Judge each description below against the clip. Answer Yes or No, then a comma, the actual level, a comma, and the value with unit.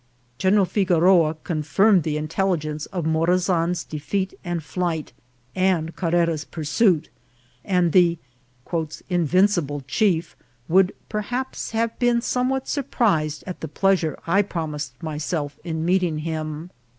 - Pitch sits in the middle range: Yes, medium, 170 Hz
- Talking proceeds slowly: Yes, slow, 120 wpm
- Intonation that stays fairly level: No, average, 3.5 semitones